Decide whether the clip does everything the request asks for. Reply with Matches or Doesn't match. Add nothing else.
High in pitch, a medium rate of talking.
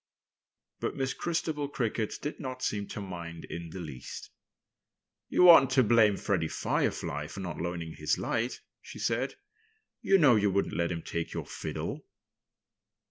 Doesn't match